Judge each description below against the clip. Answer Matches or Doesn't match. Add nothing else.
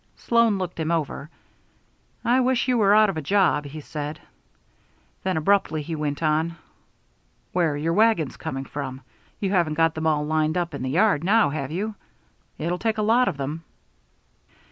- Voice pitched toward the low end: Doesn't match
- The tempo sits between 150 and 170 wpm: Doesn't match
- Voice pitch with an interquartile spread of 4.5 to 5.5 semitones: Matches